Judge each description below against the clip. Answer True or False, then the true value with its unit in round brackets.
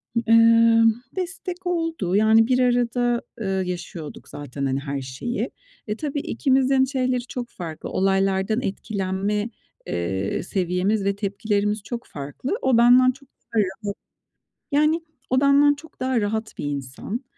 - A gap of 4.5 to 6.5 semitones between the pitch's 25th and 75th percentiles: True (5.1 semitones)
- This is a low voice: False (220 Hz)